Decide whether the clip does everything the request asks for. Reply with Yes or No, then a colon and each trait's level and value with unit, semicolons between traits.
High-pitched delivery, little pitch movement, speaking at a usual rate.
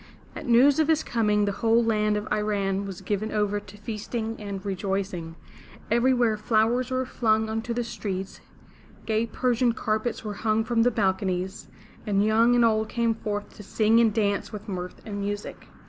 Yes: high, 215 Hz; narrow, 2.3 semitones; average, 180 wpm